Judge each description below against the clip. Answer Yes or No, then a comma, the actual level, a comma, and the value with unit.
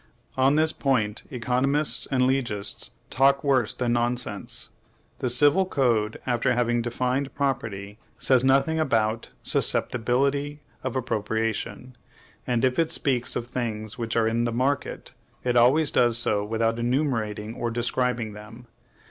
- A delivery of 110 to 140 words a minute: Yes, slow, 135 wpm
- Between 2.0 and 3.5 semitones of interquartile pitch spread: Yes, average, 2.9 semitones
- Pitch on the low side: Yes, low, 120 Hz